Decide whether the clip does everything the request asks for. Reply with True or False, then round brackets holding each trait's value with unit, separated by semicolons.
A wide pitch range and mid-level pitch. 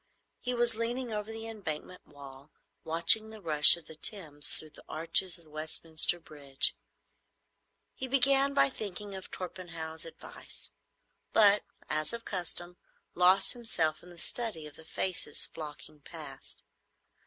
True (5.8 semitones; 175 Hz)